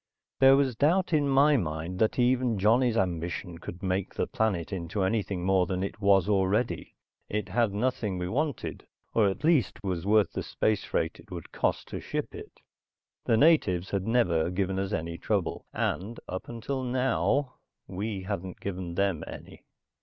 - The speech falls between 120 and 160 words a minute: No, average, 170 wpm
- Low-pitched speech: Yes, low, 100 Hz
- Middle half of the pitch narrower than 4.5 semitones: No, average, 4.8 semitones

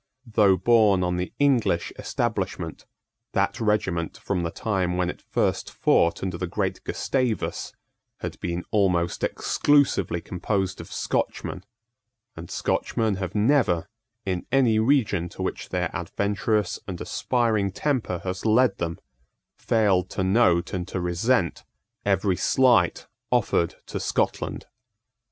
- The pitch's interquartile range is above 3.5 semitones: Yes, average, 4.0 semitones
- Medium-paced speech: No, slow, 130 wpm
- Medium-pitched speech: No, very low, 95 Hz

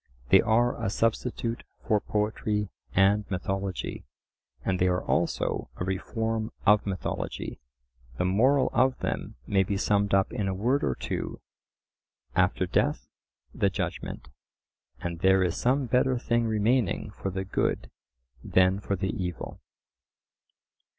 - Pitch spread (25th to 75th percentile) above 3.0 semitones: Yes, average, 3.4 semitones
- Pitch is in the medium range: No, low, 100 Hz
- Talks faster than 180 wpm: No, slow, 135 wpm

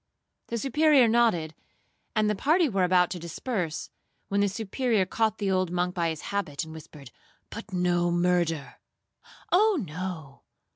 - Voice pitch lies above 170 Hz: Yes, medium, 185 Hz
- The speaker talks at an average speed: Yes, average, 145 wpm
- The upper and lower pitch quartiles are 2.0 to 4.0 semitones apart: No, average, 4.8 semitones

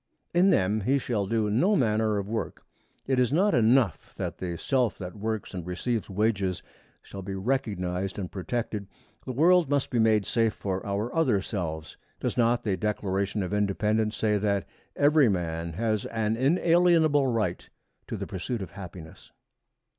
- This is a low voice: Yes, low, 110 Hz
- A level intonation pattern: No, average, 4.3 semitones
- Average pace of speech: Yes, average, 165 wpm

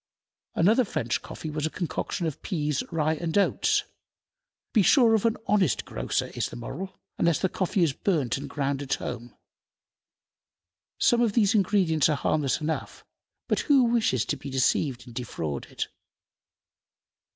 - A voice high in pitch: No, medium, 160 Hz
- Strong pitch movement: Yes, wide, 6.4 semitones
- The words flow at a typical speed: Yes, average, 150 wpm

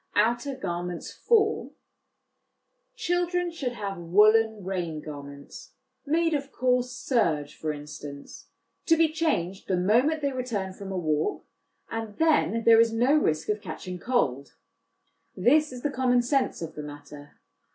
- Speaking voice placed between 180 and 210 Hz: No, high, 225 Hz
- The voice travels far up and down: Yes, wide, 8.1 semitones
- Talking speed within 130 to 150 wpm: Yes, average, 140 wpm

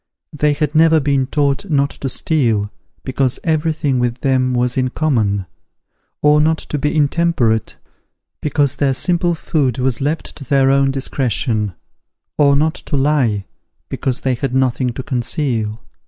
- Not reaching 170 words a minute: Yes, average, 155 wpm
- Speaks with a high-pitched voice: No, low, 135 Hz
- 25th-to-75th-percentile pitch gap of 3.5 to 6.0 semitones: No, average, 3.1 semitones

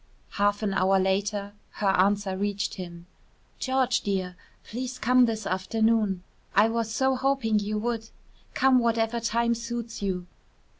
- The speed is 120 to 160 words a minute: Yes, average, 140 wpm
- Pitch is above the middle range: Yes, high, 215 Hz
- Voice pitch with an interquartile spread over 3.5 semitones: No, average, 3.0 semitones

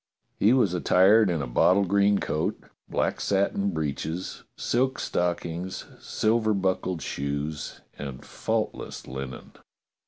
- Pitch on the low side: Yes, very low, 90 Hz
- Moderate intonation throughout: Yes, average, 4.6 semitones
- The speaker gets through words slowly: Yes, slow, 115 wpm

